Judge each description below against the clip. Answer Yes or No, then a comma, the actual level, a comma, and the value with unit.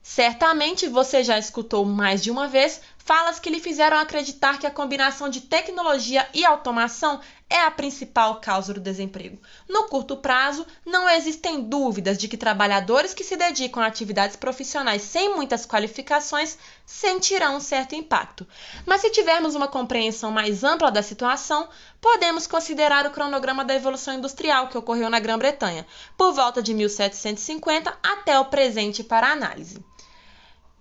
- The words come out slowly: No, average, 150 wpm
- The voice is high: Yes, very high, 275 Hz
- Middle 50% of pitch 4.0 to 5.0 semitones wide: No, wide, 5.6 semitones